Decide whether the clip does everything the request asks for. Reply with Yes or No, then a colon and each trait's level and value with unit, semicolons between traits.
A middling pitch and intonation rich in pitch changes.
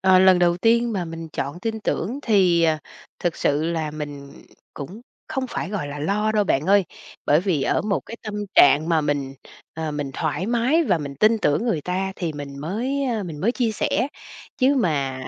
Yes: medium, 175 Hz; wide, 6.4 semitones